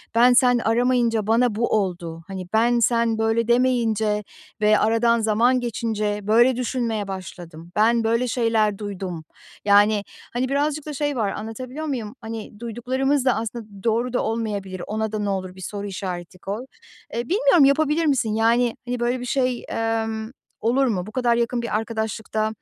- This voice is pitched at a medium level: No, high, 225 Hz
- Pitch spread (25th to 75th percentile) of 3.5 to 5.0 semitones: No, average, 2.7 semitones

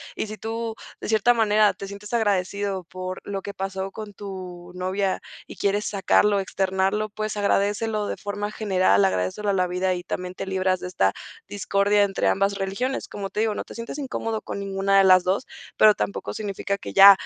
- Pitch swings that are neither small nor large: No, narrow, 1.8 semitones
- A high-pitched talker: Yes, high, 200 Hz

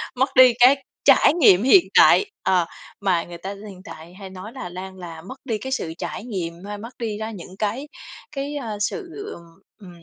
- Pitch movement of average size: No, wide, 6.1 semitones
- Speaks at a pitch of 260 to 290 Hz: No, high, 205 Hz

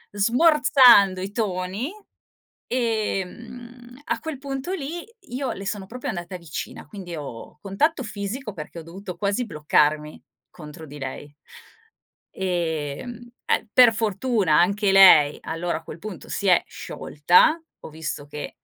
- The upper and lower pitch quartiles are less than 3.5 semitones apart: No, wide, 6.7 semitones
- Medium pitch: No, high, 195 Hz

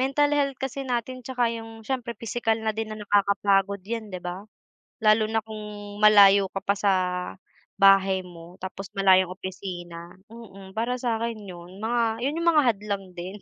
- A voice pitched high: Yes, high, 215 Hz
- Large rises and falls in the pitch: No, average, 3.2 semitones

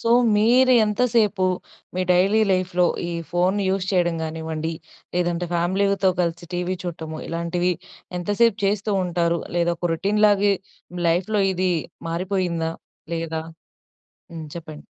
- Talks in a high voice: No, medium, 180 Hz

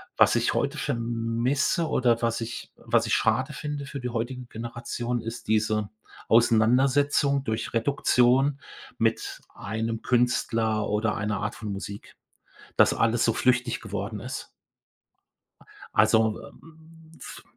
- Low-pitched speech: Yes, low, 120 Hz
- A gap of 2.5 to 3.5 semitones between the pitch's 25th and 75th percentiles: Yes, average, 2.8 semitones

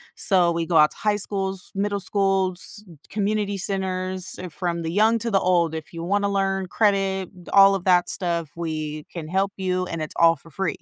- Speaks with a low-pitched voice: No, high, 190 Hz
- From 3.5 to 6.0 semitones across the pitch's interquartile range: No, narrow, 2.6 semitones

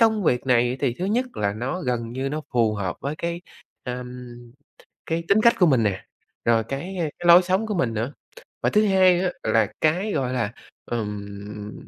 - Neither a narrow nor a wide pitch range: No, wide, 7.9 semitones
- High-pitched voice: No, low, 130 Hz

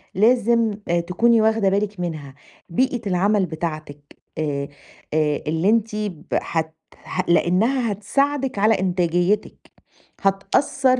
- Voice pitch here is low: No, high, 195 Hz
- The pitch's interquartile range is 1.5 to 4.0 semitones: No, average, 4.8 semitones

